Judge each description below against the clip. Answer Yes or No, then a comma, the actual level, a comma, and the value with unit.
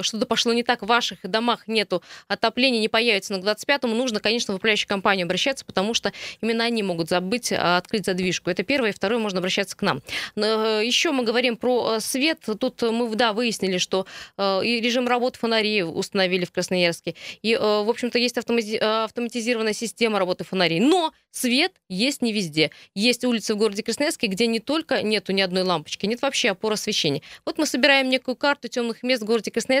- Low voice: No, high, 225 Hz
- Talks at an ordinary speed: No, fast, 185 wpm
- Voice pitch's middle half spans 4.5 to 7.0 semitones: No, average, 3.8 semitones